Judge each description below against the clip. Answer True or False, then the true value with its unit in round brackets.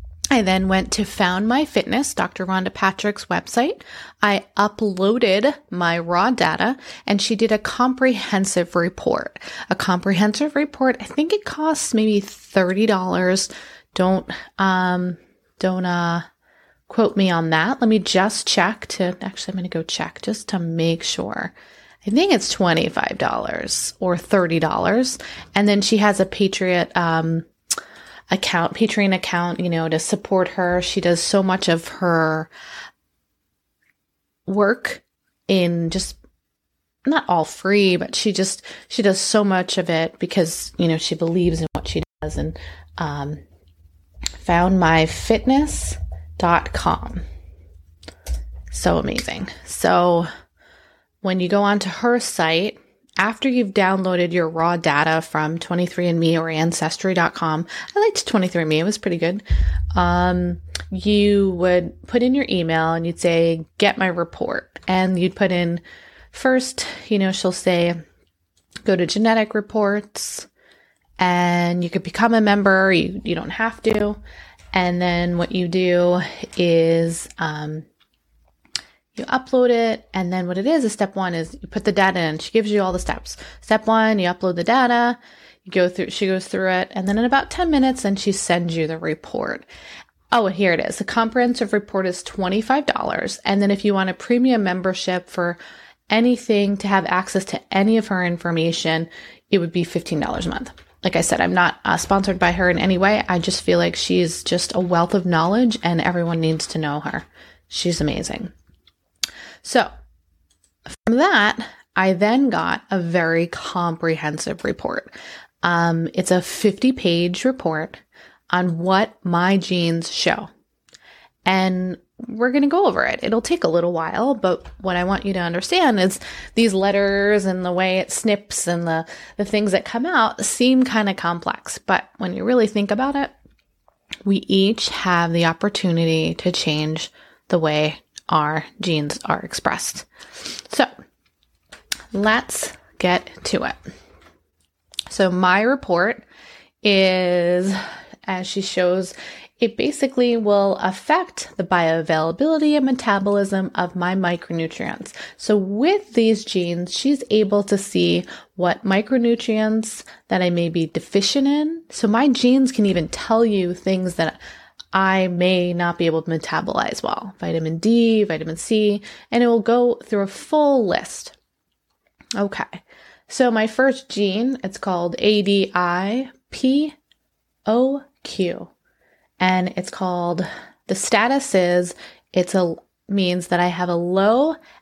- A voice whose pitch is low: False (185 Hz)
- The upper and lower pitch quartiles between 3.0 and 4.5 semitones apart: True (4.1 semitones)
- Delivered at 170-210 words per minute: False (150 wpm)